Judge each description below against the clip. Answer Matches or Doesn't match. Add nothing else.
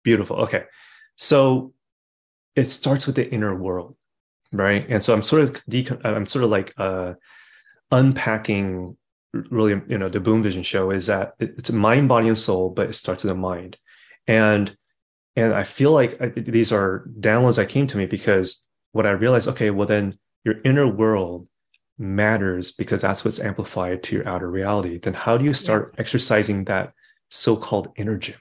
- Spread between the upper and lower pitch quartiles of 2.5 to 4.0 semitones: Doesn't match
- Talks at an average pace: Matches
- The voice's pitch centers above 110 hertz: Doesn't match